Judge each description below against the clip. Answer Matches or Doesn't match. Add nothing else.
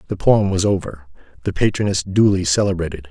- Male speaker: Matches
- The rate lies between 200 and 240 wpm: Doesn't match